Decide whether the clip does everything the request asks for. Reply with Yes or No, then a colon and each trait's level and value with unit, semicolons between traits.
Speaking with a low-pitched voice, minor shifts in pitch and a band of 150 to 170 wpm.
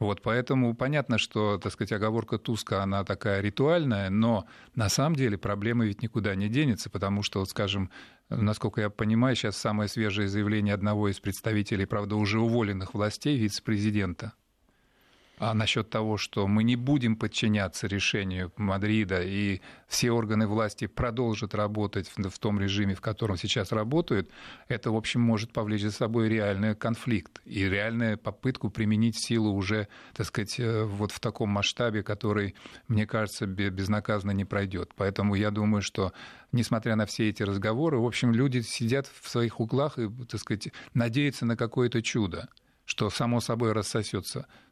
Yes: low, 110 Hz; narrow, 2.3 semitones; average, 155 wpm